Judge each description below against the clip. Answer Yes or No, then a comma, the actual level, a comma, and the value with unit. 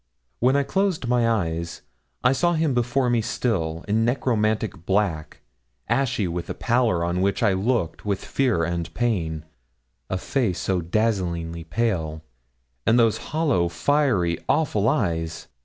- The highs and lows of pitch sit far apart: Yes, wide, 6.3 semitones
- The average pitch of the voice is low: Yes, low, 105 Hz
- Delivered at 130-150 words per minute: Yes, average, 140 wpm